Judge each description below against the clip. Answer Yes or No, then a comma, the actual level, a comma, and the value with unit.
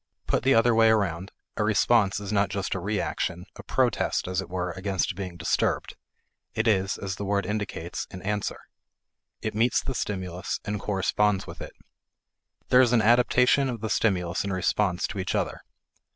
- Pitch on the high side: No, low, 100 Hz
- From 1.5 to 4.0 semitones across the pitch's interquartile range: Yes, average, 2.8 semitones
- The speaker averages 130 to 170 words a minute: No, average, 180 wpm